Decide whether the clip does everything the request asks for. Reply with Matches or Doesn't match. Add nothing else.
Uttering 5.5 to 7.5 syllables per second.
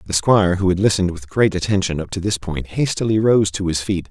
Matches